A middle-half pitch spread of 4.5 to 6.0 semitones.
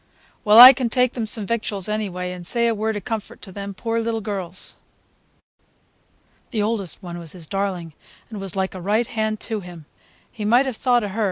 No: average, 3.2 semitones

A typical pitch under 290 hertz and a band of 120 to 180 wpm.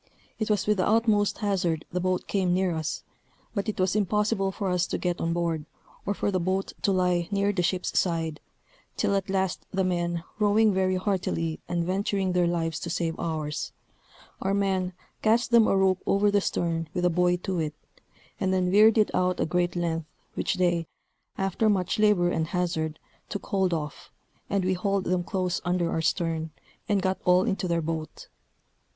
No: medium, 185 Hz; average, 190 wpm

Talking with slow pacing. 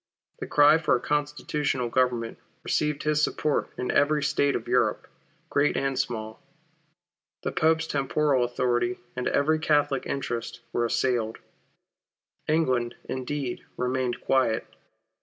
Yes: slow, 120 wpm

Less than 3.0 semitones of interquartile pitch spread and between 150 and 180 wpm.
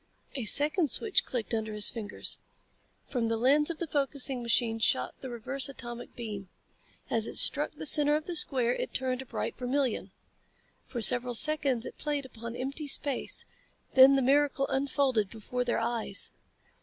No: average, 3.5 semitones; average, 170 wpm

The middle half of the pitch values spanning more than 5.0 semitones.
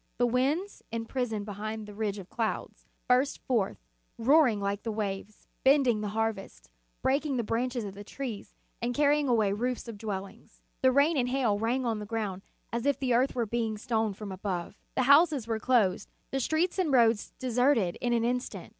No: average, 3.7 semitones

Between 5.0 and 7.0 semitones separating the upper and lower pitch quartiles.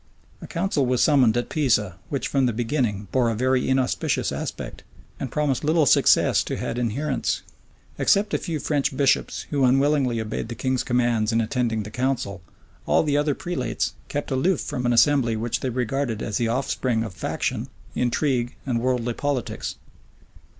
No: average, 3.4 semitones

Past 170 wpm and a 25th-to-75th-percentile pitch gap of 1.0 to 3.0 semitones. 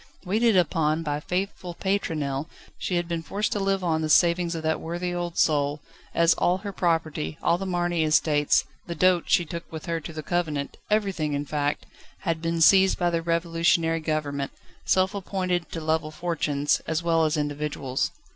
Yes: average, 180 wpm; narrow, 2.4 semitones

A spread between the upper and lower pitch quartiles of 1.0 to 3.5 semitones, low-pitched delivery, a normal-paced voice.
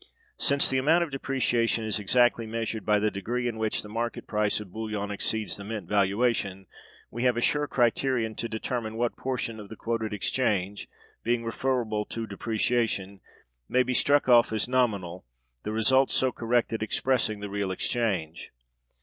Yes: average, 2.8 semitones; low, 115 Hz; average, 165 wpm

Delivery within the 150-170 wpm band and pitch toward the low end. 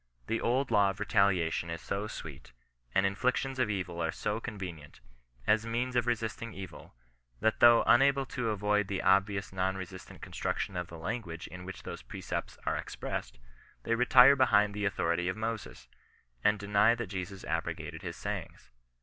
Yes: average, 165 wpm; low, 105 Hz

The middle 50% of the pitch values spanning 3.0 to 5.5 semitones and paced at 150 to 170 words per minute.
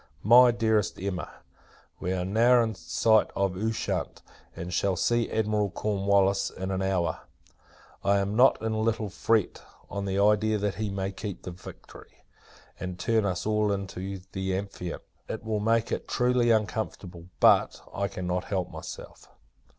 No: narrow, 2.5 semitones; average, 160 wpm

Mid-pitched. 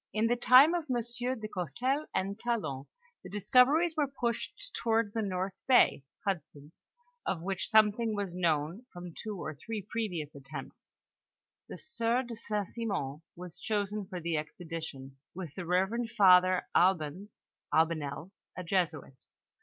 No: high, 195 Hz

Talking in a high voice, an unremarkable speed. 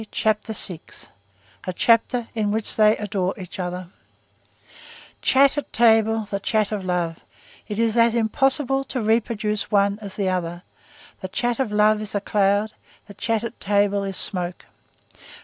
Yes: high, 210 Hz; average, 150 wpm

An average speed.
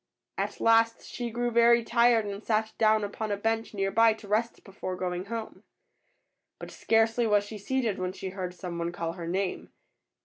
Yes: average, 190 wpm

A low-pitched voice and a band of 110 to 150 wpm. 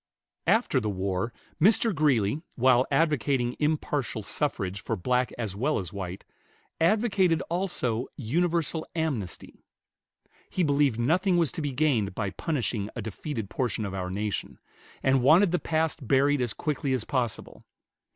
Yes: low, 130 Hz; average, 140 wpm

